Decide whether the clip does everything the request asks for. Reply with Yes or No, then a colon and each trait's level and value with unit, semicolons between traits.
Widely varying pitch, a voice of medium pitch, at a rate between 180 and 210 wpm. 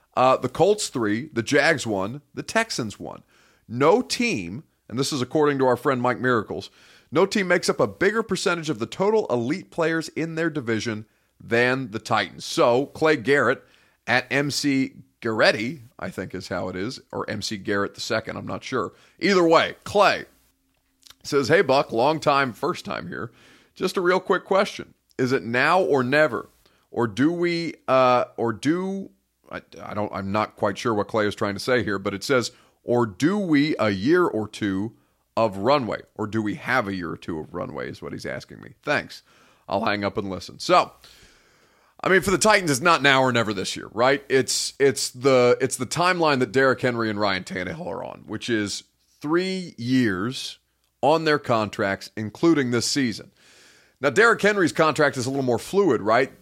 No: wide, 6.4 semitones; low, 130 Hz; average, 190 wpm